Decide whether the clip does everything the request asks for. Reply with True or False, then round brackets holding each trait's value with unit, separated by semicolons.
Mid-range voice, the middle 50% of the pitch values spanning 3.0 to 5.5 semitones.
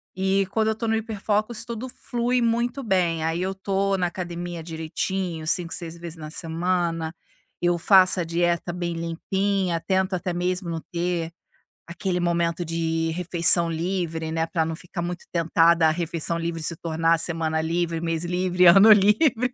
False (175 Hz; 2.5 semitones)